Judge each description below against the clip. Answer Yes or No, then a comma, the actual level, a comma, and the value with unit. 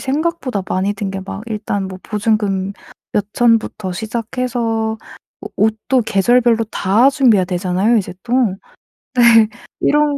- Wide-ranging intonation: No, average, 3.5 semitones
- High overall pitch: Yes, high, 220 Hz